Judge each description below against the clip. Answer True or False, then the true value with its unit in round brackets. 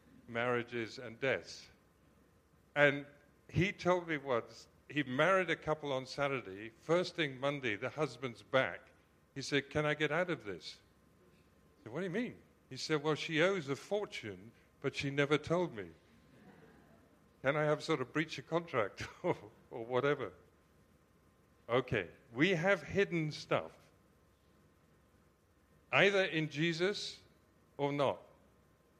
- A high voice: False (140 Hz)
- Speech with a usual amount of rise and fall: False (8.7 semitones)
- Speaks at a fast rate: False (140 wpm)